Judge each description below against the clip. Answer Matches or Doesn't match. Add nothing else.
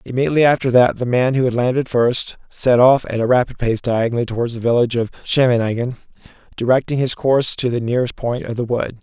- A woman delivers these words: Doesn't match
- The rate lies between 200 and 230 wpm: Matches